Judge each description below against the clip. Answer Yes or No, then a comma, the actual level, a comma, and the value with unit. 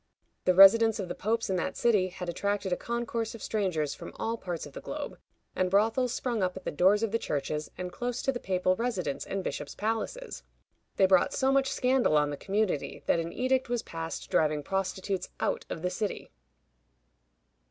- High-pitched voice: Yes, high, 195 Hz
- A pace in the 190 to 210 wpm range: Yes, average, 195 wpm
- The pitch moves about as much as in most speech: Yes, average, 4.2 semitones